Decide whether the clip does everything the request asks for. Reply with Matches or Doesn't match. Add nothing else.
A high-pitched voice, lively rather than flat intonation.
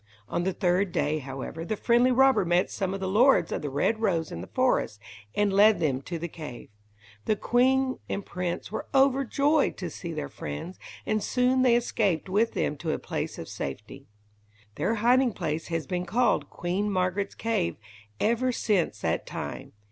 Matches